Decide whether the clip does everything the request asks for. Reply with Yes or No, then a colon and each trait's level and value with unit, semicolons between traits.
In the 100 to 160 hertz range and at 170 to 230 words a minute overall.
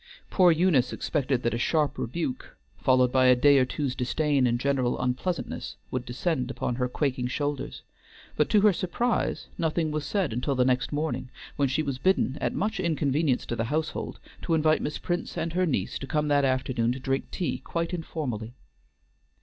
Yes: medium, 140 Hz; average, 185 wpm